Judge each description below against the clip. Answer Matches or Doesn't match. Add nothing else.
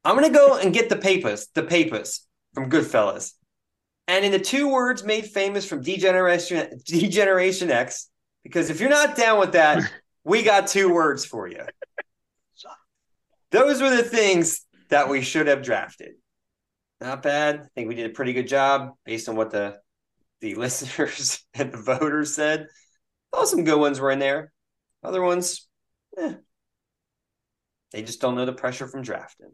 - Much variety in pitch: Matches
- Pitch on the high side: Doesn't match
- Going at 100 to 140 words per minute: Doesn't match